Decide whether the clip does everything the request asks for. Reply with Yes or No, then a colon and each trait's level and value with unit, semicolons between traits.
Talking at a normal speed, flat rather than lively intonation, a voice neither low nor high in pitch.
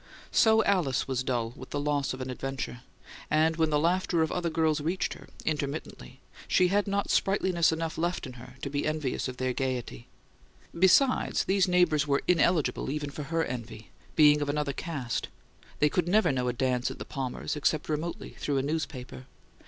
No: average, 185 wpm; average, 4.3 semitones; medium, 150 Hz